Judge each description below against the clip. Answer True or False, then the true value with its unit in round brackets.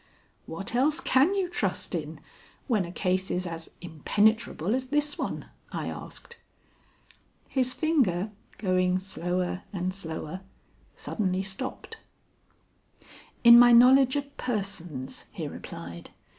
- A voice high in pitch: True (195 Hz)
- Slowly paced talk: True (115 wpm)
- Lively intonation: True (6.2 semitones)